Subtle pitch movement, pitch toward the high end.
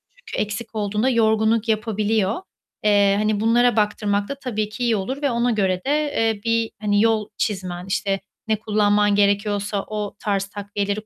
Yes: narrow, 1.9 semitones; high, 210 Hz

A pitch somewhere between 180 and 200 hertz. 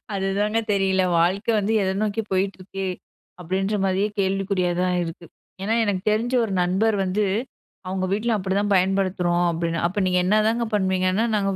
Yes: high, 195 Hz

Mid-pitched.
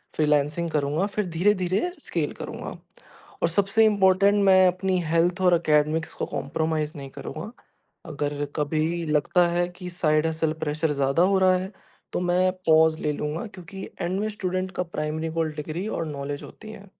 Yes: medium, 165 Hz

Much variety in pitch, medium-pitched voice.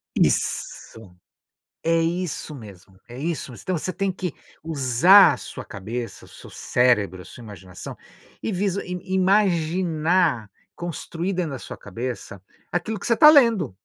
Yes: wide, 7.7 semitones; medium, 165 Hz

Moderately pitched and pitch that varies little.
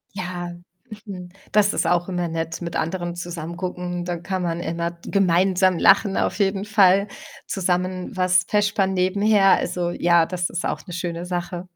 Yes: medium, 180 Hz; narrow, 1.7 semitones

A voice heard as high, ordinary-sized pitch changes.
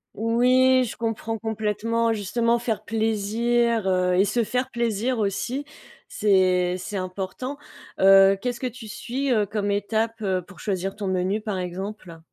Yes: high, 215 Hz; average, 3.3 semitones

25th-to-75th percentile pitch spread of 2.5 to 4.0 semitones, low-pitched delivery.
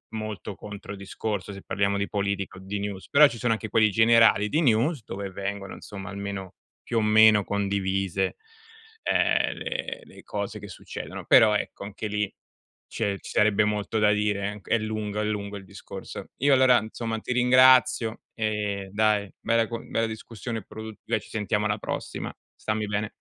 No: narrow, 1.8 semitones; low, 105 Hz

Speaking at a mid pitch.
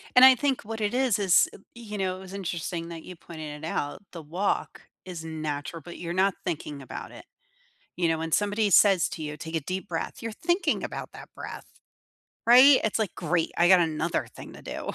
Yes: medium, 180 Hz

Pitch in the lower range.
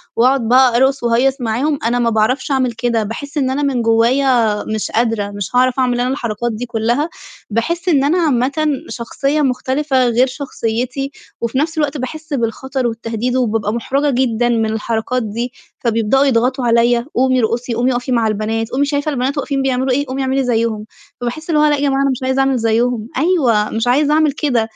No: very high, 250 Hz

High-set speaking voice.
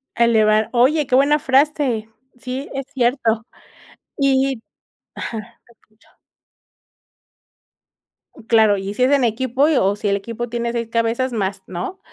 Yes: high, 235 Hz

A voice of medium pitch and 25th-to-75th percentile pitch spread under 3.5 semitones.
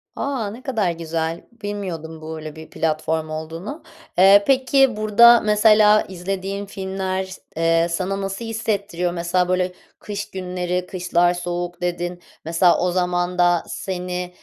Yes: medium, 180 Hz; average, 2.8 semitones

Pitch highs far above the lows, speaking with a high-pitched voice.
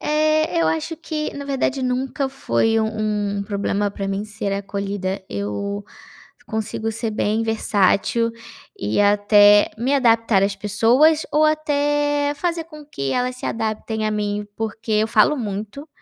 Yes: wide, 5.7 semitones; high, 225 Hz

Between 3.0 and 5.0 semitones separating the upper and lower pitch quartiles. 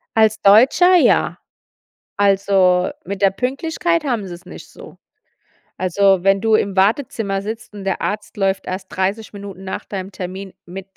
No: narrow, 2.4 semitones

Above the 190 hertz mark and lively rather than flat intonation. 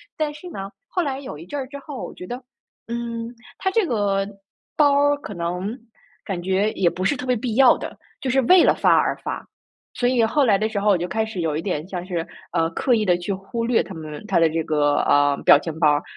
Yes: high, 210 Hz; wide, 6.6 semitones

